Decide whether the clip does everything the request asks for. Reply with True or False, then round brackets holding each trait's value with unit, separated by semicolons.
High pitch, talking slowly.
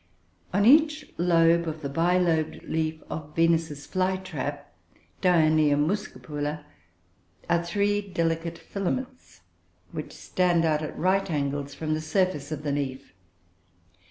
False (165 Hz; 125 wpm)